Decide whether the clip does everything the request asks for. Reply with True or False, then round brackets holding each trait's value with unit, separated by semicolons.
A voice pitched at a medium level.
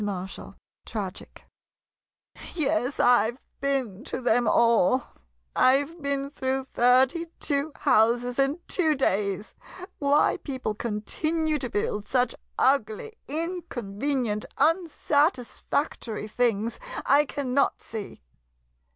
False (255 Hz)